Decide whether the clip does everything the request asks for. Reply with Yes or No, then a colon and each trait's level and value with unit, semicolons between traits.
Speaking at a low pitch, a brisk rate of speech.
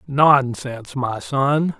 No: low, 130 Hz; slow, 100 wpm